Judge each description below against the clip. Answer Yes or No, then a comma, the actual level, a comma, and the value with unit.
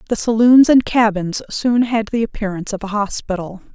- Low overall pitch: No, high, 215 Hz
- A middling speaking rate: Yes, average, 175 wpm